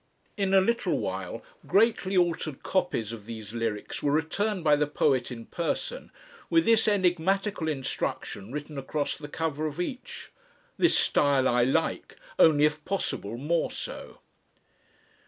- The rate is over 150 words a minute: No, average, 140 wpm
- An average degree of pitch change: No, wide, 6.1 semitones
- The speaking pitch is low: No, medium, 155 Hz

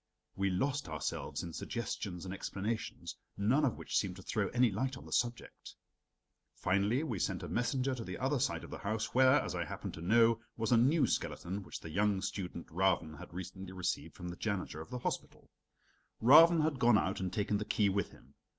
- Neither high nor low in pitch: No, low, 105 Hz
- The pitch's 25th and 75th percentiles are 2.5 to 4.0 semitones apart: No, average, 4.8 semitones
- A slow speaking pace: No, fast, 205 wpm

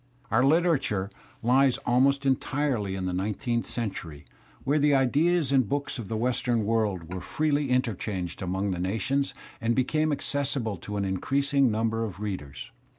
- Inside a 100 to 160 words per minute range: Yes, average, 150 wpm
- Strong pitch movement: Yes, wide, 5.7 semitones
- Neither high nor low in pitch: No, low, 120 Hz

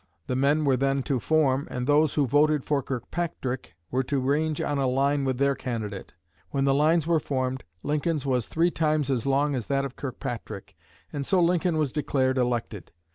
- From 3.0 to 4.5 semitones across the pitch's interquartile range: No, narrow, 2.6 semitones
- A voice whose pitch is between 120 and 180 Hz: Yes, medium, 140 Hz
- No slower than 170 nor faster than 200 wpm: Yes, average, 190 wpm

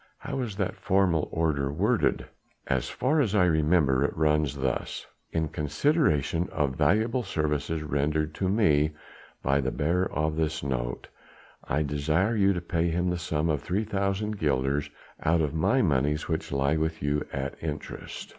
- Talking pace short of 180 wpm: Yes, average, 160 wpm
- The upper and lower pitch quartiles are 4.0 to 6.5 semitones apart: Yes, average, 4.3 semitones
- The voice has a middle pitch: No, very low, 80 Hz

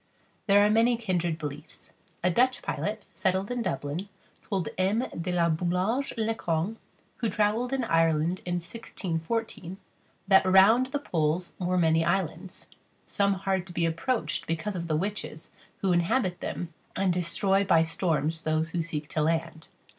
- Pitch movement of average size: Yes, average, 3.8 semitones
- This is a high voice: No, medium, 180 Hz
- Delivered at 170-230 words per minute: No, average, 155 wpm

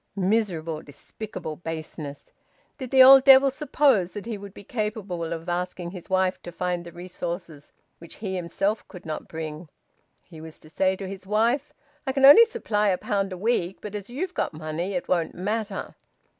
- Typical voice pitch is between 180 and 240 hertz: Yes, high, 190 Hz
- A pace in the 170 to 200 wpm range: Yes, average, 185 wpm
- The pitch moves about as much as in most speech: Yes, average, 4.3 semitones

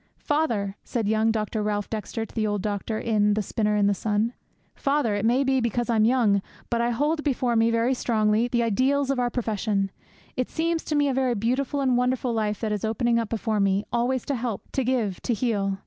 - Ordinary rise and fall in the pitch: Yes, average, 3.1 semitones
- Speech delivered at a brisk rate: Yes, fast, 220 wpm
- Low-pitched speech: No, high, 230 Hz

